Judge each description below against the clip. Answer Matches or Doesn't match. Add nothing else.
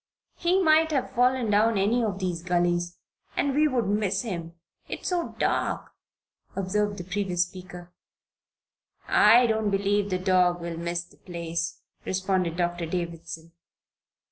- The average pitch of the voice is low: Doesn't match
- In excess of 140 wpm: Doesn't match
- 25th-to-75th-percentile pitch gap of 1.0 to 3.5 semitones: Doesn't match